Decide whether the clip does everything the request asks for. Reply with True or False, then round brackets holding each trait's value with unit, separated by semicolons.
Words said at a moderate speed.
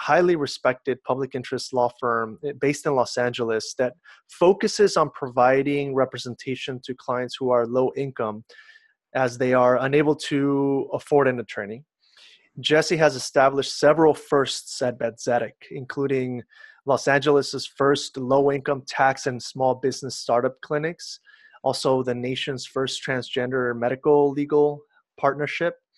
False (130 wpm)